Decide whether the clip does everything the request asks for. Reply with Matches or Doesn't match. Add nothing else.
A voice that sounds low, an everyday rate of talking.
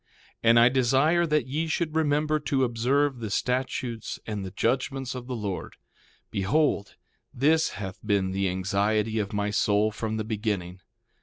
Matches